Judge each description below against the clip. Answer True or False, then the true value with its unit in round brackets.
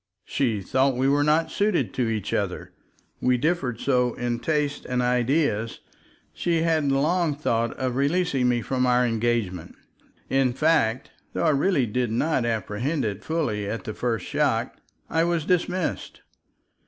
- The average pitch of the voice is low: True (130 Hz)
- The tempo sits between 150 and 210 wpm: True (155 wpm)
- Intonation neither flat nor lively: True (4.8 semitones)